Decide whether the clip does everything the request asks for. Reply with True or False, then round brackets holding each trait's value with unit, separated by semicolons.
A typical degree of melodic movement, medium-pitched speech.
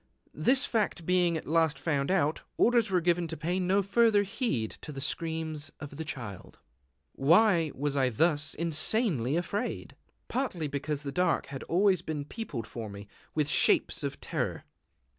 True (4.7 semitones; 160 Hz)